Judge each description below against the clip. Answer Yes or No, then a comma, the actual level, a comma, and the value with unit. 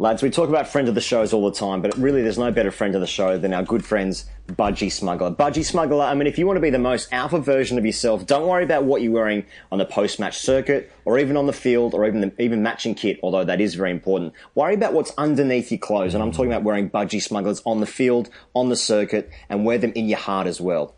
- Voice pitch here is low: Yes, low, 115 Hz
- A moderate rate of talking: No, fast, 270 wpm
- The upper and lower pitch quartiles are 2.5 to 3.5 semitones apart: No, average, 4.7 semitones